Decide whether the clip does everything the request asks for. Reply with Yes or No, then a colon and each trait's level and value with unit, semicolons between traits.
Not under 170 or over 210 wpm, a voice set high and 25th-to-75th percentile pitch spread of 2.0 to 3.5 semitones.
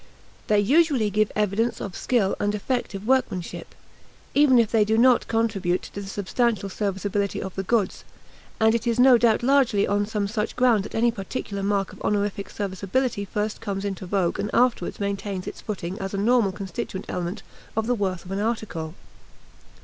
Yes: average, 180 wpm; high, 205 Hz; average, 2.9 semitones